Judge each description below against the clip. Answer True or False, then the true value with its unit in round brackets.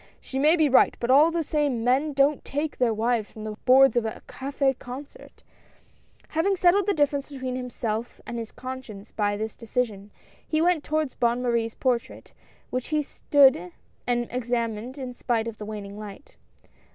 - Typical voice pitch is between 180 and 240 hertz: False (250 Hz)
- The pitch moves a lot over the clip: False (4.0 semitones)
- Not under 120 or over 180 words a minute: True (175 wpm)